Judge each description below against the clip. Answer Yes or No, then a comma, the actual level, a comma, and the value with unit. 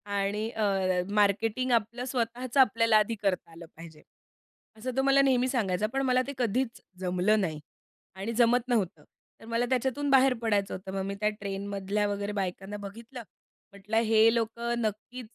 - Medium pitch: No, high, 220 Hz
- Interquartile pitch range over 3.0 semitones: Yes, average, 3.6 semitones